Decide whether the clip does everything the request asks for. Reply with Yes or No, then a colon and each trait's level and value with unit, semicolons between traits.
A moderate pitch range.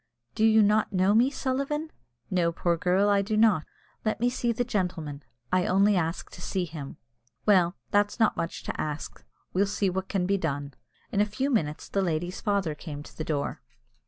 Yes: average, 4.2 semitones